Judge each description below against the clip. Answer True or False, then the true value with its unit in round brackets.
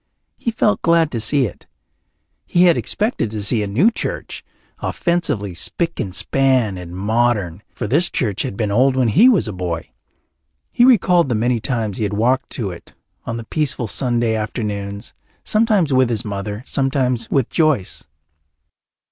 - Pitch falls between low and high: False (120 Hz)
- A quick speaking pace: False (165 wpm)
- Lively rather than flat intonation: True (6.2 semitones)